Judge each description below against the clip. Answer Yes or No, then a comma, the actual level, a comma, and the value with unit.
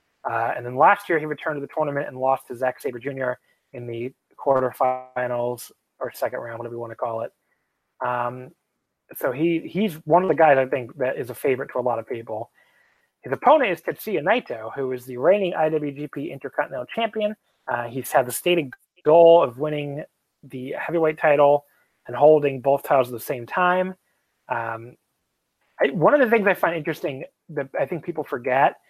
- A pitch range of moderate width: Yes, average, 4.7 semitones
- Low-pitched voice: No, medium, 145 Hz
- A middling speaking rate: Yes, average, 190 wpm